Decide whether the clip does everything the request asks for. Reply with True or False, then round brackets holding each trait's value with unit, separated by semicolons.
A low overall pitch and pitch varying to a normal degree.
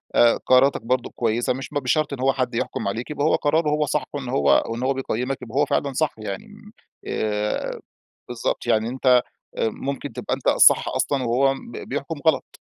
True (130 Hz; 3.1 semitones)